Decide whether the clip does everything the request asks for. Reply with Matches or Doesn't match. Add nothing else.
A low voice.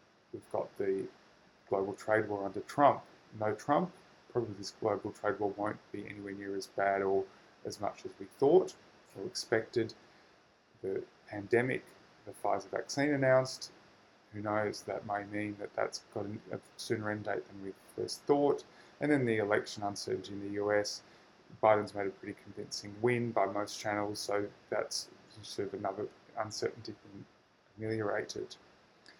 Matches